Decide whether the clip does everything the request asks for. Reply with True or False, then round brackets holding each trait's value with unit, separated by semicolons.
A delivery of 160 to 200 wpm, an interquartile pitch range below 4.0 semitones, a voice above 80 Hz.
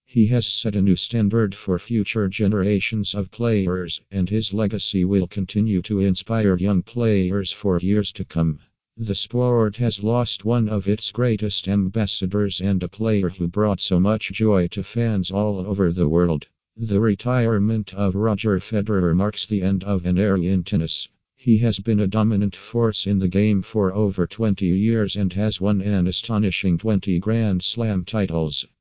True (170 wpm; 2.5 semitones; 100 Hz)